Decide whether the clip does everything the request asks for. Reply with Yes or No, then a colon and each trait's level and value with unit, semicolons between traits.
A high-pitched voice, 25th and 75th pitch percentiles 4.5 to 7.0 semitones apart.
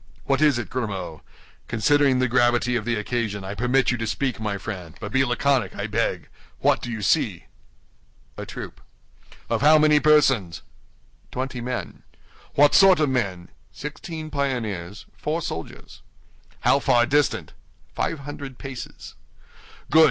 No: low, 125 Hz; average, 4.9 semitones